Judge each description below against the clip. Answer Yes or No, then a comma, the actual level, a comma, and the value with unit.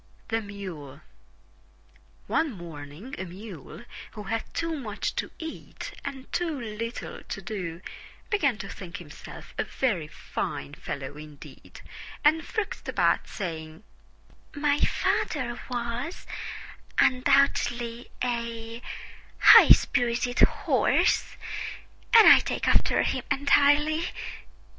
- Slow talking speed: Yes, slow, 105 wpm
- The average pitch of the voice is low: No, high, 230 Hz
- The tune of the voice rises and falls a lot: Yes, wide, 7.4 semitones